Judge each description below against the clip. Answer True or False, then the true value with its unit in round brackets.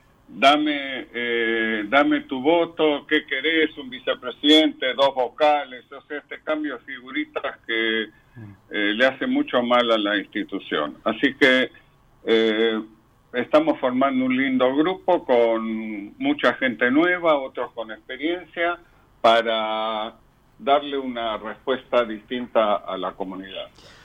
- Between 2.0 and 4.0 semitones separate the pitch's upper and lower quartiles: False (5.1 semitones)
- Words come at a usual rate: False (120 wpm)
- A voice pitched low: True (130 Hz)